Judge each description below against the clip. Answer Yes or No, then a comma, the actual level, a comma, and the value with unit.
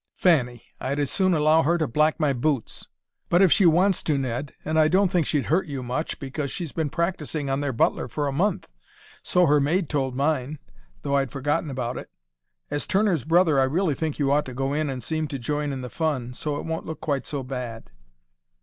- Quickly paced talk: Yes, fast, 225 wpm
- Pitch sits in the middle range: Yes, medium, 150 Hz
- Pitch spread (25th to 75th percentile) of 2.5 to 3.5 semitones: Yes, average, 3.2 semitones